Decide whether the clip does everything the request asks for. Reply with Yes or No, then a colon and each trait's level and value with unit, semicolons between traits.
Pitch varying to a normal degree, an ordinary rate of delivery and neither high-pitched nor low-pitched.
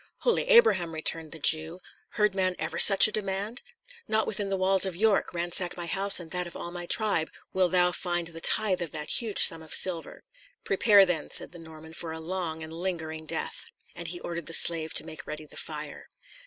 No: average, 3.0 semitones; fast, 210 wpm; medium, 175 Hz